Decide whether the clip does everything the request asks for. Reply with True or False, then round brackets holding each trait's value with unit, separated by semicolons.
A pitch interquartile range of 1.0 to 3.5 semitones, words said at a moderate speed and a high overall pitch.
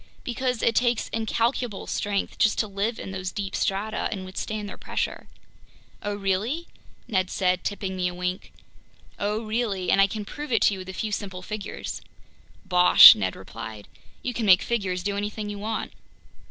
True (2.7 semitones; 180 wpm; 205 Hz)